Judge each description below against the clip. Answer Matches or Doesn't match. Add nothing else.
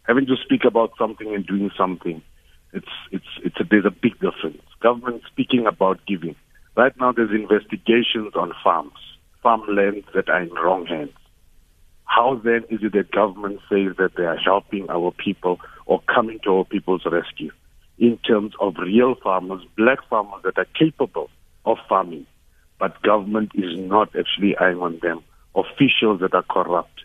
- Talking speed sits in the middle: Matches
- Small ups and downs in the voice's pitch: Doesn't match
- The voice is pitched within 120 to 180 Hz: Doesn't match